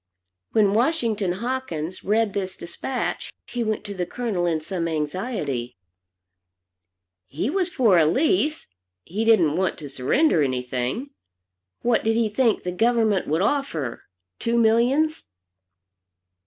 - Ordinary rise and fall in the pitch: No, wide, 6.4 semitones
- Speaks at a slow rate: Yes, slow, 130 wpm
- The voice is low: No, high, 210 Hz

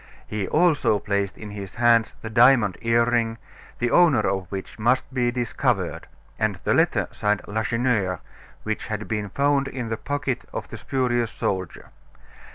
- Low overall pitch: Yes, low, 115 Hz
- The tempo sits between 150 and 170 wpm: Yes, average, 155 wpm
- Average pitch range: Yes, average, 3.1 semitones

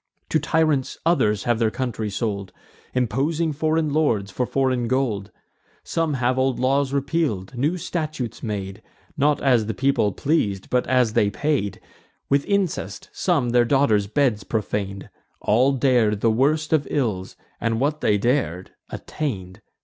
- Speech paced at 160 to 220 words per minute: No, average, 145 wpm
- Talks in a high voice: No, low, 125 Hz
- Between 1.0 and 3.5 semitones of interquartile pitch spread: No, average, 5.3 semitones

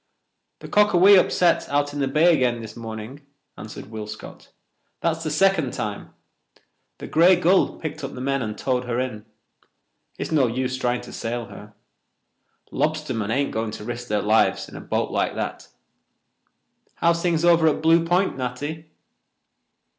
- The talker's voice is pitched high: No, low, 135 Hz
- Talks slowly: No, average, 160 wpm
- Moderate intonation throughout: No, wide, 5.8 semitones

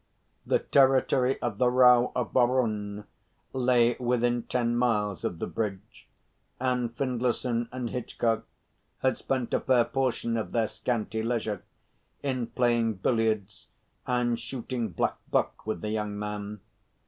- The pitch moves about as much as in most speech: No, narrow, 2.3 semitones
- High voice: No, low, 120 Hz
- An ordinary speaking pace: No, slow, 130 wpm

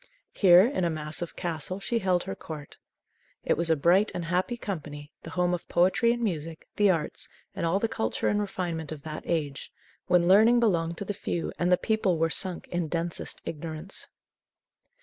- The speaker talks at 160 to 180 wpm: No, average, 190 wpm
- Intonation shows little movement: No, average, 3.1 semitones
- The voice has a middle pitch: Yes, medium, 175 Hz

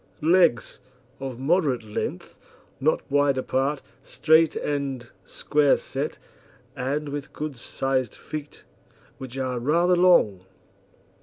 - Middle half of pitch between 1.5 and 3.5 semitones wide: Yes, average, 2.7 semitones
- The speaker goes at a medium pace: No, slow, 105 wpm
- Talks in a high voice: No, medium, 140 Hz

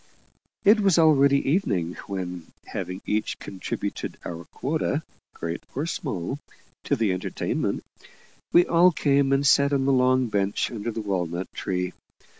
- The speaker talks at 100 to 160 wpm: Yes, average, 140 wpm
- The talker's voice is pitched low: Yes, low, 120 Hz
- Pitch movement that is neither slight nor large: No, wide, 7.4 semitones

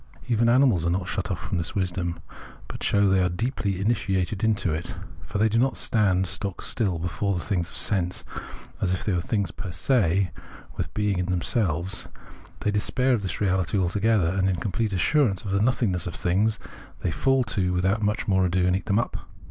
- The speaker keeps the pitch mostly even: No, average, 3.1 semitones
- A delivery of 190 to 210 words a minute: Yes, average, 200 wpm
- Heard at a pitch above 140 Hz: No, very low, 95 Hz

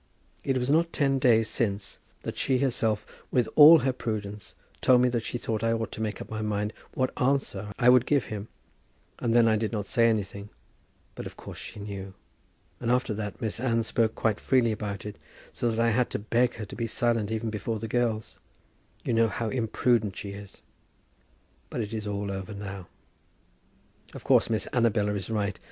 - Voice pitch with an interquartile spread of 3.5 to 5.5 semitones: No, narrow, 2.6 semitones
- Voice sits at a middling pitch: No, low, 110 Hz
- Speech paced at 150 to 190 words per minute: No, average, 200 wpm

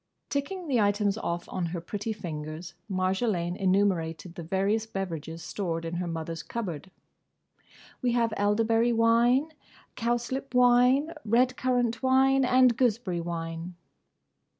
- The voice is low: No, high, 205 Hz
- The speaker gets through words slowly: Yes, slow, 125 wpm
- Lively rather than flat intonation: Yes, wide, 6.0 semitones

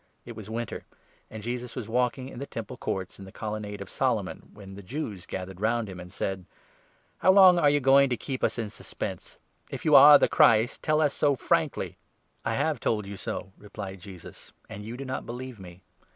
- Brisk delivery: Yes, fast, 225 wpm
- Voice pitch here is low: Yes, low, 115 Hz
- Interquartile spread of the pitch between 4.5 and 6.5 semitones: Yes, average, 5.0 semitones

